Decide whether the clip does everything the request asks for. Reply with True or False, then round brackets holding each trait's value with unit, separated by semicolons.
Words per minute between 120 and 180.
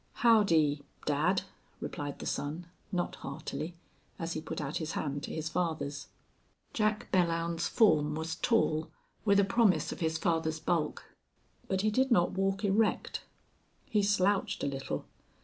True (150 wpm)